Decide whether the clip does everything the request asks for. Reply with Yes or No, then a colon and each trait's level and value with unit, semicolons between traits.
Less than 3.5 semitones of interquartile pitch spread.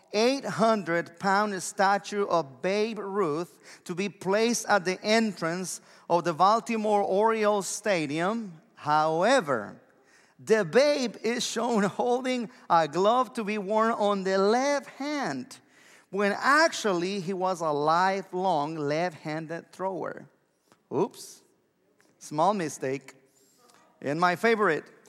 No: average, 4.3 semitones